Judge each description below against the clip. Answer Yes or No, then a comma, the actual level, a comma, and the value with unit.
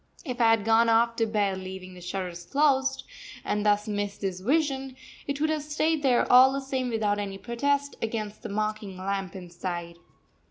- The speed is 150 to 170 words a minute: No, average, 185 wpm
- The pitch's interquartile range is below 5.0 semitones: No, wide, 5.4 semitones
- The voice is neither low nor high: No, high, 220 Hz